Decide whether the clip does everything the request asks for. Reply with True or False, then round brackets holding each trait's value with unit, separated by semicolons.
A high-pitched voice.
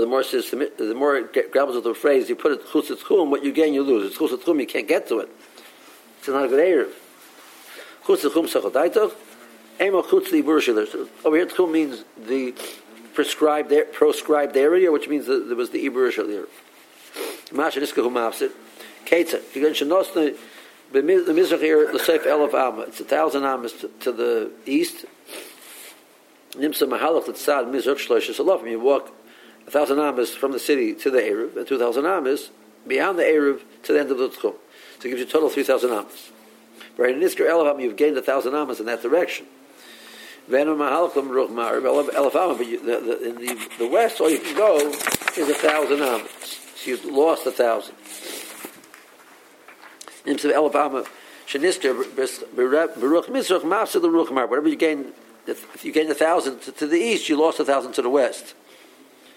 True (370 Hz)